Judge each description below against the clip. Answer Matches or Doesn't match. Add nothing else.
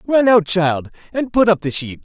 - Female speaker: Doesn't match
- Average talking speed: Doesn't match